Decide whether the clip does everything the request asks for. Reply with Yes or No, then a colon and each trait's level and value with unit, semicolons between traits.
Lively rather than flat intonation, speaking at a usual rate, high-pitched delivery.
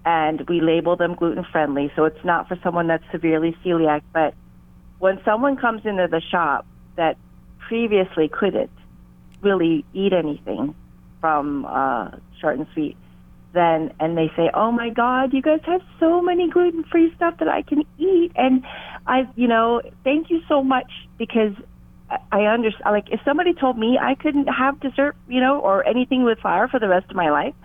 Yes: wide, 8.6 semitones; average, 180 wpm; high, 200 Hz